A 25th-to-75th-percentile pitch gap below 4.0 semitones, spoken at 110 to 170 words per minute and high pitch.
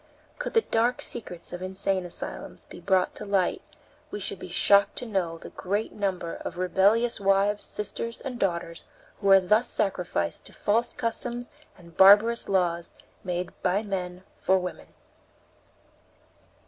Yes: average, 3.1 semitones; average, 150 wpm; high, 195 Hz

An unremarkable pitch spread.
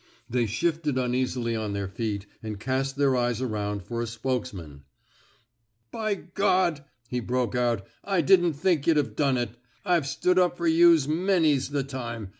No: wide, 5.8 semitones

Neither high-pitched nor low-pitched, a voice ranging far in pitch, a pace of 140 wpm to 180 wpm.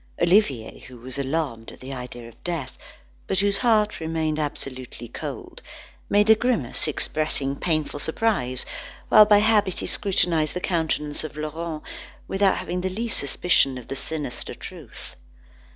Yes: medium, 155 Hz; wide, 6.0 semitones; average, 150 wpm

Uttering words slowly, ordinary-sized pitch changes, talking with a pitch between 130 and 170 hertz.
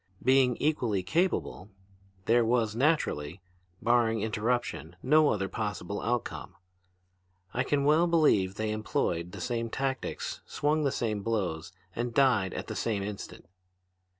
No: slow, 130 wpm; average, 4.6 semitones; low, 115 Hz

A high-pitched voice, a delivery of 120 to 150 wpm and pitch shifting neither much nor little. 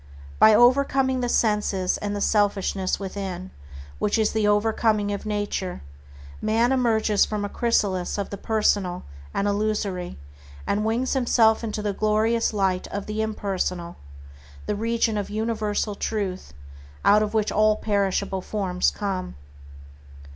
No: high, 210 Hz; slow, 135 wpm; narrow, 1.8 semitones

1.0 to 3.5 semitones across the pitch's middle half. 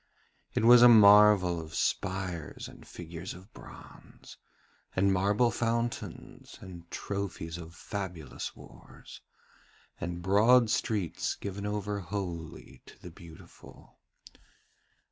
Yes: average, 3.2 semitones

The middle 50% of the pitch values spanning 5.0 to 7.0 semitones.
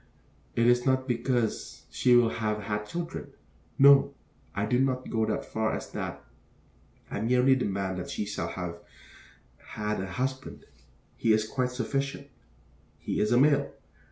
No: average, 3.6 semitones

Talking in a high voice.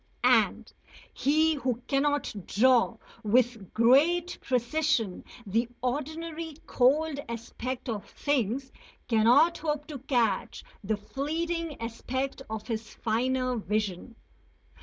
Yes: very high, 255 Hz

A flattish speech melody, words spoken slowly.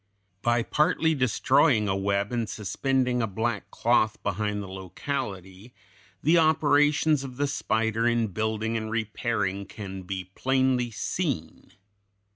No: average, 4.5 semitones; slow, 125 wpm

